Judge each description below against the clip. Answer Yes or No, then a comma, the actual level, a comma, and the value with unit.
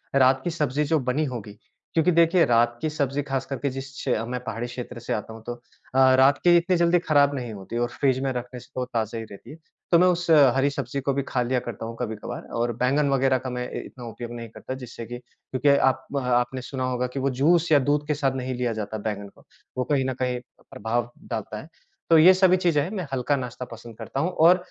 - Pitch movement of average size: Yes, average, 3.2 semitones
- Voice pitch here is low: Yes, low, 130 Hz